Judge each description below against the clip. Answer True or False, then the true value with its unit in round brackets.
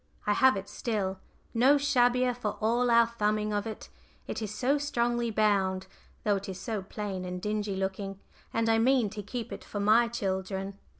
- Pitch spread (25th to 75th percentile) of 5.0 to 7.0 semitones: False (3.2 semitones)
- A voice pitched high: True (215 Hz)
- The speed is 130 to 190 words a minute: True (185 wpm)